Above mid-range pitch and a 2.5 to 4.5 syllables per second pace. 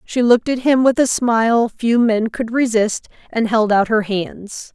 Yes: high, 230 Hz; 4.3 syllables/s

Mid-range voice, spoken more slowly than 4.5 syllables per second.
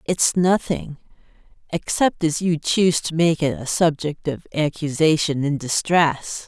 Yes: medium, 155 Hz; 4.2 syllables/s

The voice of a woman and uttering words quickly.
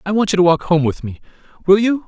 No: male; fast, 260 wpm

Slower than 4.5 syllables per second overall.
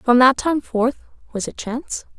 No: 4.6 syllables/s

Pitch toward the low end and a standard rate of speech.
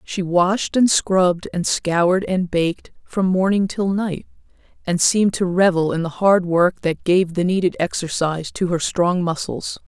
No: medium, 180 Hz; average, 175 wpm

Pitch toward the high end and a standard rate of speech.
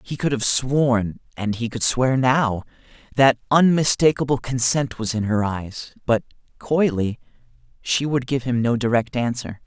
No: low, 125 Hz; average, 155 wpm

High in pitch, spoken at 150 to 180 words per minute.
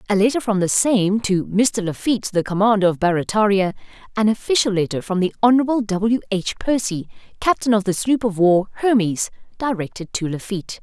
Yes: high, 205 Hz; average, 170 wpm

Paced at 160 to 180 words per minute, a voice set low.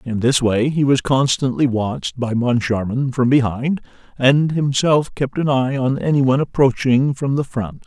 Yes: average, 175 wpm; low, 130 Hz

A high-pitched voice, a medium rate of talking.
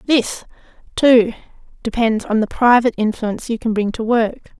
Yes: high, 225 Hz; average, 155 wpm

